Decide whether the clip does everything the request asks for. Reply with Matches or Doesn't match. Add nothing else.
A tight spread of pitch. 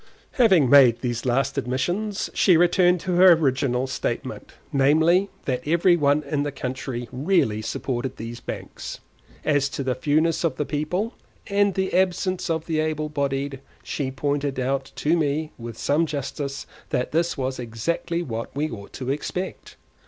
Doesn't match